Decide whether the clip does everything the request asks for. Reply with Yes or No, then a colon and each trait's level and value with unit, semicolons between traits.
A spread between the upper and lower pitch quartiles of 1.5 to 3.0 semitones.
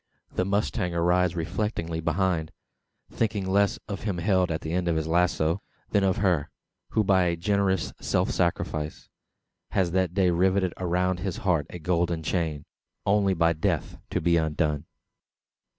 Yes: narrow, 2.4 semitones